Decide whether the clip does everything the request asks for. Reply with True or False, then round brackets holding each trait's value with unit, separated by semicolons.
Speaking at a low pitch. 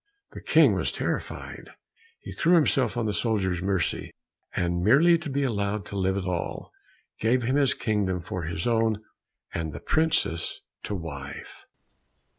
True (105 Hz)